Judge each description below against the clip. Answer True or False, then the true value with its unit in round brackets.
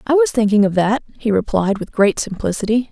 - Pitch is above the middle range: True (220 Hz)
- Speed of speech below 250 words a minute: True (205 wpm)